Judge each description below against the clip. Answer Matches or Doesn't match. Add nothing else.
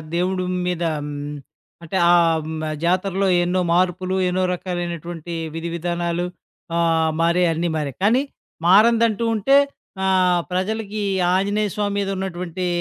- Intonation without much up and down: Matches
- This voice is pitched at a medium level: Matches